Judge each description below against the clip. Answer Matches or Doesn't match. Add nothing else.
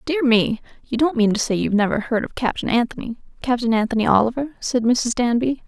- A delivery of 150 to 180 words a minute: Doesn't match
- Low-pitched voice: Doesn't match